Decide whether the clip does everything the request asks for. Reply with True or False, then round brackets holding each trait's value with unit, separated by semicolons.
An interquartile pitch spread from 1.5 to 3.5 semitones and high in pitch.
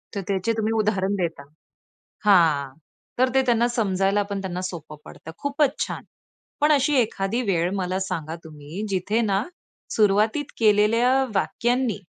False (4.0 semitones; 200 Hz)